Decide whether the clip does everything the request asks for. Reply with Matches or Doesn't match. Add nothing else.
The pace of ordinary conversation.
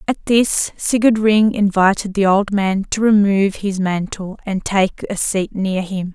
Matches